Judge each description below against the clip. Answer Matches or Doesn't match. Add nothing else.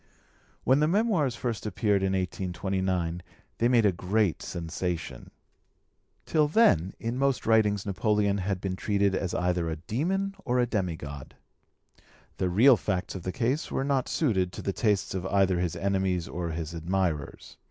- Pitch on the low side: Matches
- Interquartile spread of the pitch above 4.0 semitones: Matches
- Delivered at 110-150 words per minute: Doesn't match